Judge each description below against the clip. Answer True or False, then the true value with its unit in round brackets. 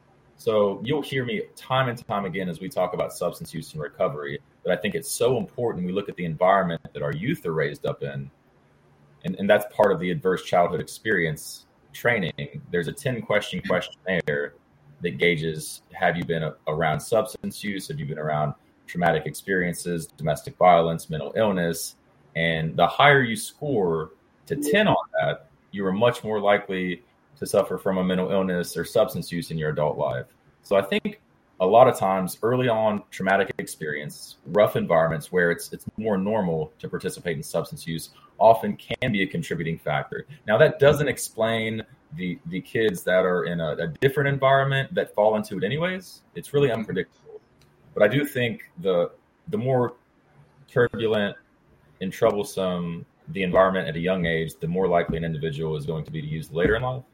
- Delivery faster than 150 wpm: True (185 wpm)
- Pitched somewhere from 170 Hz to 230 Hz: False (95 Hz)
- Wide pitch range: True (7.7 semitones)